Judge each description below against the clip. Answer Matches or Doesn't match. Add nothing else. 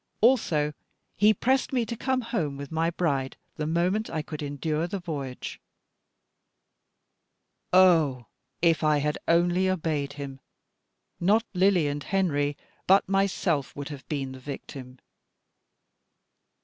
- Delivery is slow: Matches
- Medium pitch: Matches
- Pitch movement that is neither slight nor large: Matches